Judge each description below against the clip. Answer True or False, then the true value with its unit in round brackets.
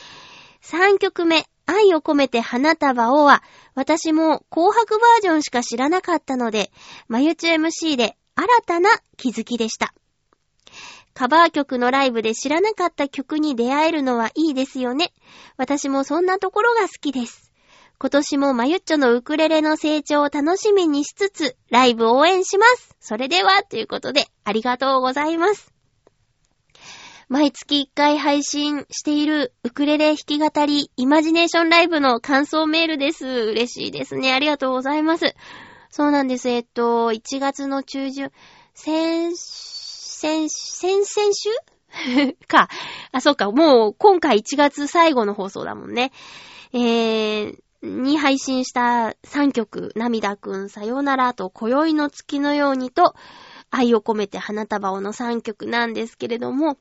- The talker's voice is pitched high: True (285 Hz)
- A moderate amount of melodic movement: True (4.6 semitones)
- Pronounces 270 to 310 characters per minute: True (290 characters per minute)